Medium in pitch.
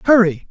No: high, 200 Hz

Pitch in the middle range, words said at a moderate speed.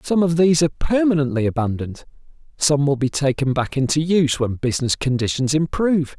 Yes: medium, 145 Hz; average, 165 wpm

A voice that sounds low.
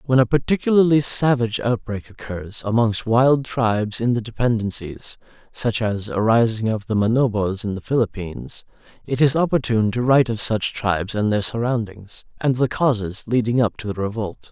Yes: low, 115 Hz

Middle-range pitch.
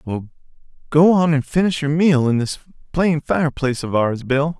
Yes: medium, 145 Hz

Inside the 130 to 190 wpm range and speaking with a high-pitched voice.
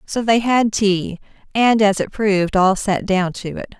No: fast, 205 wpm; high, 205 Hz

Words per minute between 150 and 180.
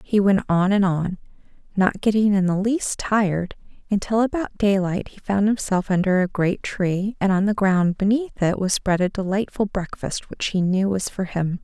No: average, 195 wpm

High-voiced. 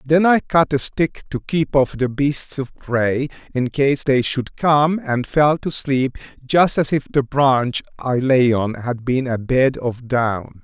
No: low, 135 Hz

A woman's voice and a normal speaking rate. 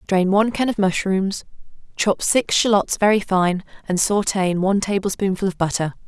Yes: female; average, 170 wpm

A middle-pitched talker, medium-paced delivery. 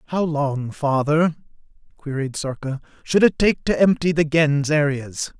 Yes: medium, 150 Hz; average, 145 wpm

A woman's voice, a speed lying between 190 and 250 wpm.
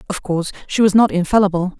Yes: female; average, 200 wpm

